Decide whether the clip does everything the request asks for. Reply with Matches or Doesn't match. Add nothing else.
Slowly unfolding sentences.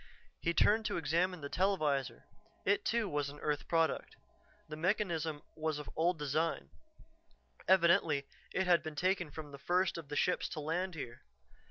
Doesn't match